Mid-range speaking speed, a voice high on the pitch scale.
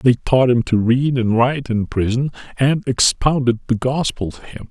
No: average, 190 wpm; low, 125 Hz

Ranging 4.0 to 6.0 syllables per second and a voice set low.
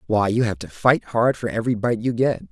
Yes: 5.5 syllables/s; low, 115 Hz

